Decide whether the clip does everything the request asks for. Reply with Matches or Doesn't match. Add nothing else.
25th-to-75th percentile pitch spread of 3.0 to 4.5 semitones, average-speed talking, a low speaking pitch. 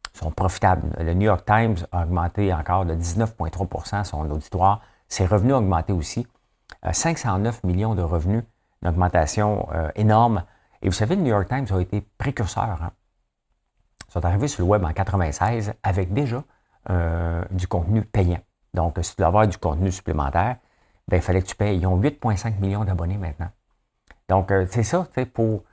Matches